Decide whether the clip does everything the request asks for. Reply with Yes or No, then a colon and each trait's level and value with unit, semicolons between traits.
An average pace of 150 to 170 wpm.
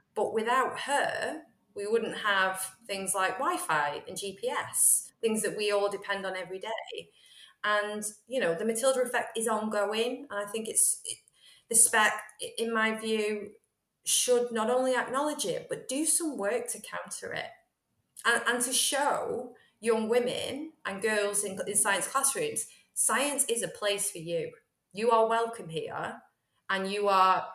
Yes: average, 160 wpm